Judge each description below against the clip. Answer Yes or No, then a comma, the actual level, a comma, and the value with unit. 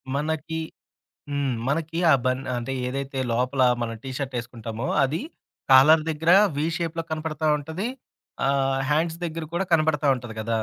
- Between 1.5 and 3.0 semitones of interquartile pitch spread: No, average, 3.5 semitones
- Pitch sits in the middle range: Yes, medium, 145 Hz